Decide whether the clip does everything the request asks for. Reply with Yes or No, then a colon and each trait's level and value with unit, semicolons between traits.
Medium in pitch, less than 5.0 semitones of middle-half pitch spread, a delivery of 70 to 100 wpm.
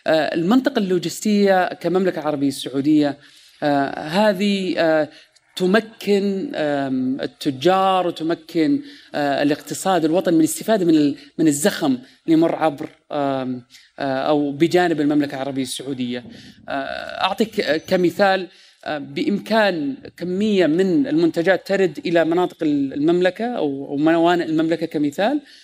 No: medium, 175 Hz; wide, 5.6 semitones; average, 85 wpm